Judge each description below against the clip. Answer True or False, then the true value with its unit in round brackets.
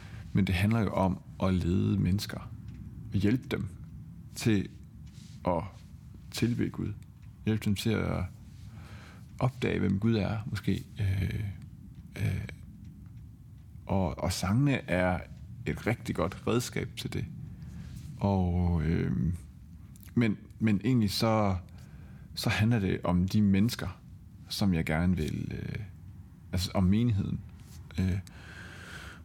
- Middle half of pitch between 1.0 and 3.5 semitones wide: True (3.0 semitones)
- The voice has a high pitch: False (100 Hz)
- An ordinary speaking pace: False (115 wpm)